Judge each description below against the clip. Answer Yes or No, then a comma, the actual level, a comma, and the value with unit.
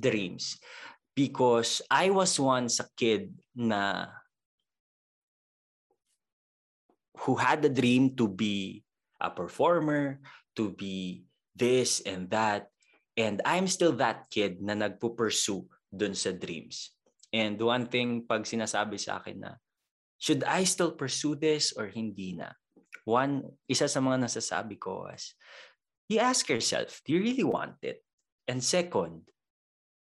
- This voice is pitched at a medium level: No, low, 120 Hz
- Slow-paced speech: Yes, slow, 125 wpm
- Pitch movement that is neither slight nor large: No, wide, 5.7 semitones